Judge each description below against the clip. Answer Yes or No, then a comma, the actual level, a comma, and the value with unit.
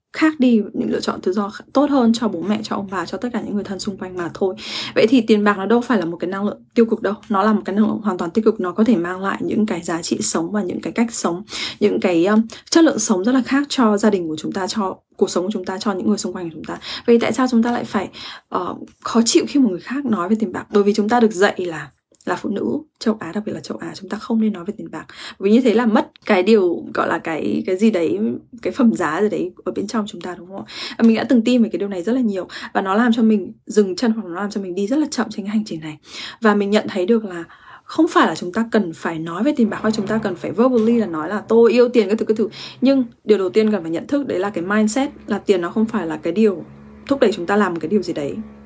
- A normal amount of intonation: Yes, average, 3.6 semitones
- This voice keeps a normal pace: No, fast, 320 wpm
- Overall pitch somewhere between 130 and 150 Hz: No, high, 215 Hz